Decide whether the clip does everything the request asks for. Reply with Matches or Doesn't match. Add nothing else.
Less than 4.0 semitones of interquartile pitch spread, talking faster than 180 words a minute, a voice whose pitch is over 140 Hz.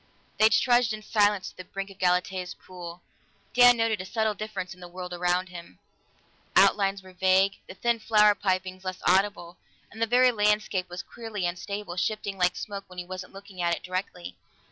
Matches